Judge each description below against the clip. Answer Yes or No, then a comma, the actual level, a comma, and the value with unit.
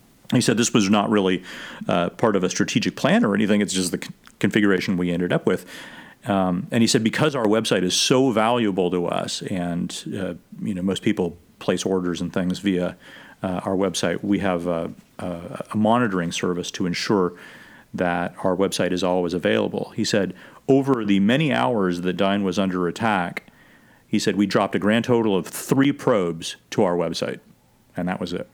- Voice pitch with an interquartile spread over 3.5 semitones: No, average, 3.0 semitones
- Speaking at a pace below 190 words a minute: No, average, 195 wpm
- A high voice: No, very low, 95 Hz